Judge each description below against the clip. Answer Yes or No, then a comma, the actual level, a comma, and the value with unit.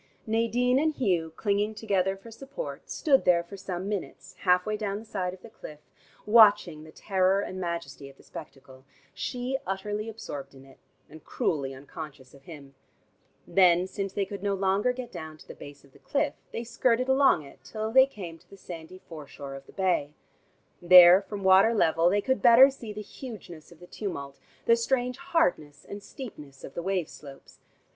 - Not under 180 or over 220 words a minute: Yes, average, 190 wpm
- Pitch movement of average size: No, wide, 5.8 semitones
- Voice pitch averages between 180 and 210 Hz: Yes, high, 190 Hz